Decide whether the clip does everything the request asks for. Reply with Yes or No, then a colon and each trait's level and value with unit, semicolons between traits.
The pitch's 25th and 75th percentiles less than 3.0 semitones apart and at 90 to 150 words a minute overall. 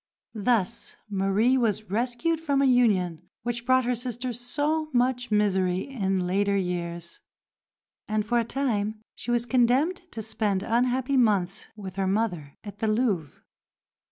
No: average, 4.2 semitones; average, 145 wpm